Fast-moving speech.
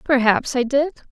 No: average, 160 wpm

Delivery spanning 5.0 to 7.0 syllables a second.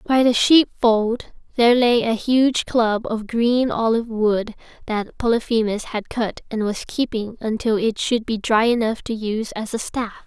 No: 4.5 syllables/s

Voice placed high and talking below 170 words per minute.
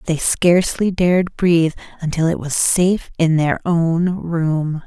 No: medium, 170 Hz; average, 150 wpm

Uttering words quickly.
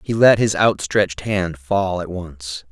No: average, 175 wpm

